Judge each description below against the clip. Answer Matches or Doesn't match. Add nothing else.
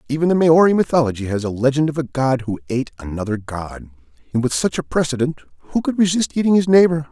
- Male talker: Matches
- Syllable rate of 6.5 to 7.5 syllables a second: Matches